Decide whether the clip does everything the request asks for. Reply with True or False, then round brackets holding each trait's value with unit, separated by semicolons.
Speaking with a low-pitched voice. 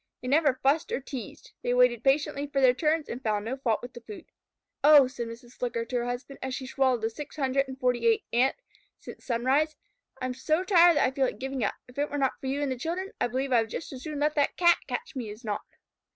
False (265 Hz)